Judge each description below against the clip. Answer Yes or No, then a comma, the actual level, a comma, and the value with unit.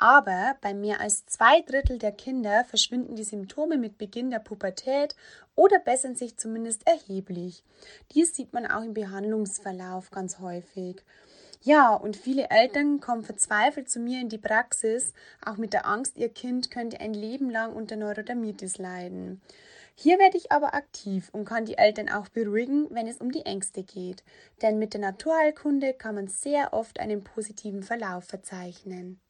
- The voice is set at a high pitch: Yes, high, 220 Hz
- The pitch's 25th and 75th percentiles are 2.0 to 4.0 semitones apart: No, average, 4.4 semitones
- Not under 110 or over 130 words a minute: No, average, 165 wpm